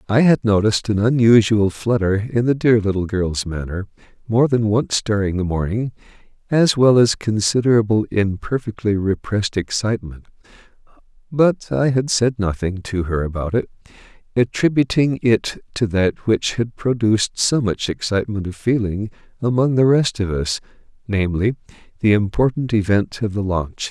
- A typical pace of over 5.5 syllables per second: No, 4.9 syllables/s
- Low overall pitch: Yes, low, 110 Hz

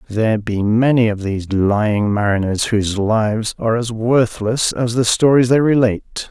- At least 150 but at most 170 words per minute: Yes, average, 160 wpm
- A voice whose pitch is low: Yes, low, 110 Hz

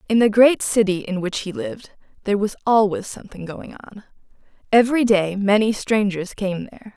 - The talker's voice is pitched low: No, high, 210 Hz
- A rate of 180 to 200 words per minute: No, average, 170 wpm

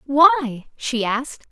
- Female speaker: Yes, female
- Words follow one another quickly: No, slow, 120 wpm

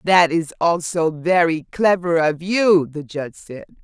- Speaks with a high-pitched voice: No, medium, 170 Hz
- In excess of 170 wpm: No, average, 155 wpm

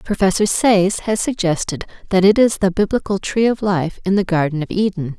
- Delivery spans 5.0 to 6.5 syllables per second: Yes, 5.4 syllables/s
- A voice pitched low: No, high, 190 Hz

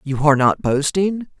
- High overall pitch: No, medium, 155 Hz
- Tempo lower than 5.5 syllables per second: Yes, 5.0 syllables/s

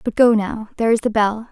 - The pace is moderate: No, fast, 280 wpm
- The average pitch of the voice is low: No, high, 220 Hz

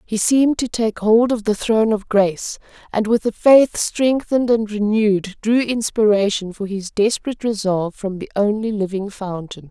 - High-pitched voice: Yes, high, 215 Hz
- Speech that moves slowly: No, average, 175 wpm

